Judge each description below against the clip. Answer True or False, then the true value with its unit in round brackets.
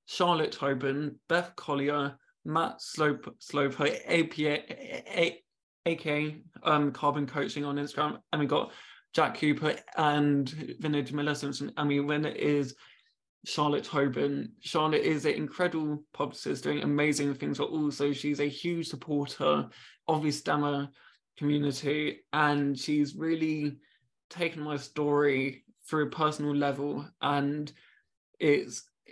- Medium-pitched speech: True (145 Hz)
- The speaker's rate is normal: False (130 wpm)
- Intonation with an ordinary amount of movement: False (1.1 semitones)